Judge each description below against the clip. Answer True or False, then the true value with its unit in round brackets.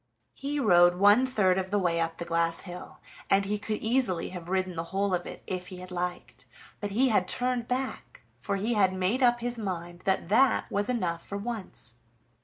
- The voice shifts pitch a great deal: False (4.2 semitones)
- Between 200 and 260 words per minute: True (205 wpm)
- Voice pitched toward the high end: True (195 Hz)